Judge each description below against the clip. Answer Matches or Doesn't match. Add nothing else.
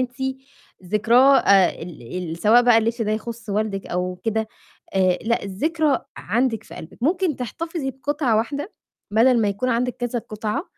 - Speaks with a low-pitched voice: Doesn't match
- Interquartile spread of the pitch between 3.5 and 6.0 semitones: Matches